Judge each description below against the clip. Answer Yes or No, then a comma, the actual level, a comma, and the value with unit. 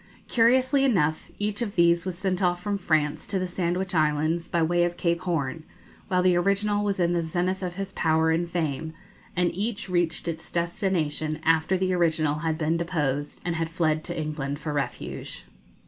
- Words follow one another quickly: No, average, 185 wpm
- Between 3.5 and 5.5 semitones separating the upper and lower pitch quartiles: No, average, 2.8 semitones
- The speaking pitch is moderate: Yes, medium, 170 Hz